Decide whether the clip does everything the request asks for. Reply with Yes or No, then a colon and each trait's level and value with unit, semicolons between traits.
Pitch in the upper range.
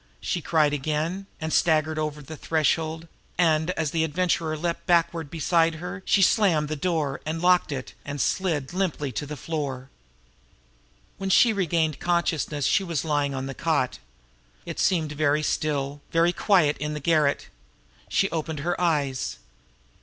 No: medium, 155 Hz